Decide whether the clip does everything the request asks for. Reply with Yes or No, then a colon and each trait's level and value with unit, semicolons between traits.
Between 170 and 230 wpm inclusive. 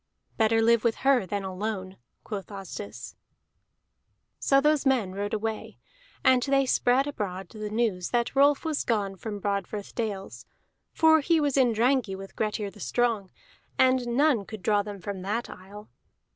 No: average, 160 wpm